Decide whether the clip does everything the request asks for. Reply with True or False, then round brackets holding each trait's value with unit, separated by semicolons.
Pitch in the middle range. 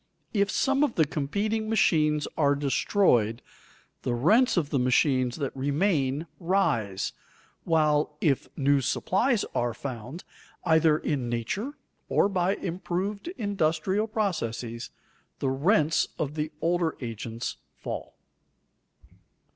True (155 Hz)